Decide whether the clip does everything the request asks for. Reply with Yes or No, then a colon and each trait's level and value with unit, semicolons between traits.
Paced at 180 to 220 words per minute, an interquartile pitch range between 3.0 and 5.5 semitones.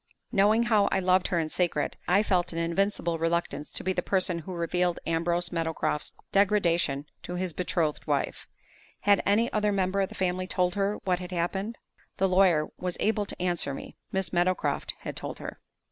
No: average, 185 wpm; narrow, 2.4 semitones